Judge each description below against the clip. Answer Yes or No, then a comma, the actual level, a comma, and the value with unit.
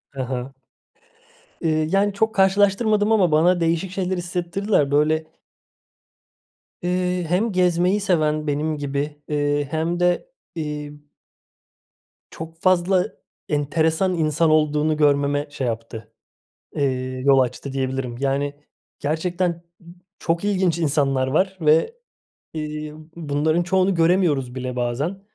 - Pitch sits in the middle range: Yes, medium, 155 Hz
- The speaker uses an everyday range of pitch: Yes, average, 3.9 semitones